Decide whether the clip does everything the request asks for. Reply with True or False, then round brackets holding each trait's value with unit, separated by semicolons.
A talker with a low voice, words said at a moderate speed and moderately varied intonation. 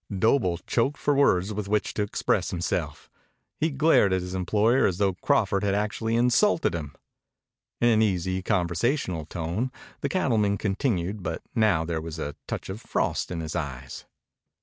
True (100 Hz; 165 wpm; 4.6 semitones)